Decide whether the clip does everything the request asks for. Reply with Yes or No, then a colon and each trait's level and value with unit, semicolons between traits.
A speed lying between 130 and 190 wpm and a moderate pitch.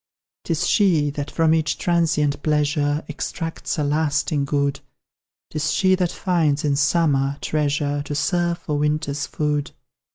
Yes: slow, 135 wpm; medium, 150 Hz